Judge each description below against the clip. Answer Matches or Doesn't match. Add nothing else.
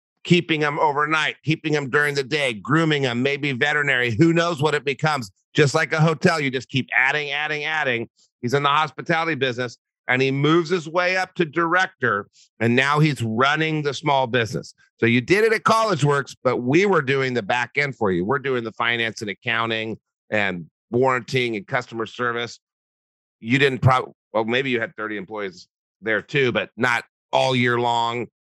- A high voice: Doesn't match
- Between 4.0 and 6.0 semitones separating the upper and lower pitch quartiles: Matches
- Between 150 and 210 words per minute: Matches